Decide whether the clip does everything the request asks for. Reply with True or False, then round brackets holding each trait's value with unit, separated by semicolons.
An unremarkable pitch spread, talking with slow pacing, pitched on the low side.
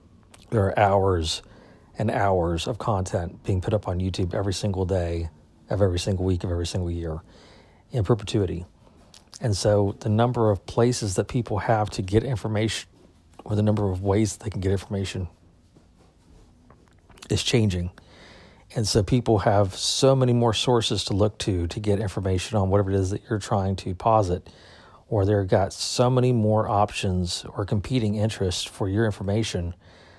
False (3.3 semitones; 170 wpm; 100 Hz)